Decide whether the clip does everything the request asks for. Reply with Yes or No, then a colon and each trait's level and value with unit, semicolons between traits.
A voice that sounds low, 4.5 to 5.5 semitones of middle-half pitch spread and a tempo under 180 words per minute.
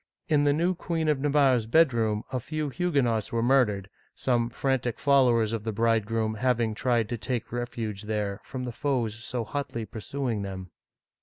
No: low, 120 Hz; average, 3.8 semitones; average, 170 wpm